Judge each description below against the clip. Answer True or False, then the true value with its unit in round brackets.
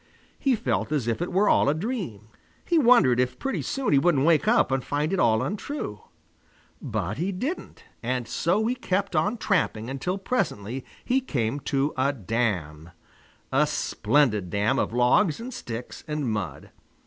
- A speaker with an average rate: True (170 wpm)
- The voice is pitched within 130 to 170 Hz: True (140 Hz)